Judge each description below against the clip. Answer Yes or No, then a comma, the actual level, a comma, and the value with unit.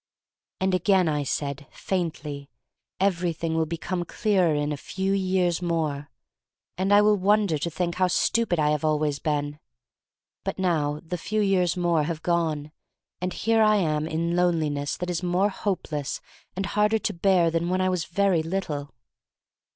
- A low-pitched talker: No, medium, 170 Hz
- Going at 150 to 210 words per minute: Yes, average, 175 wpm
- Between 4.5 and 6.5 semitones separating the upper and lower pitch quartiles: No, average, 3.7 semitones